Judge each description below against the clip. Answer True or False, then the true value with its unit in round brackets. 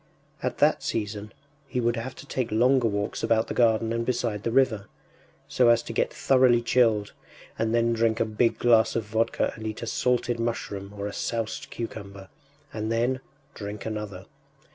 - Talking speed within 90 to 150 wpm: False (180 wpm)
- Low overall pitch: True (115 Hz)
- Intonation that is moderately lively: False (1.8 semitones)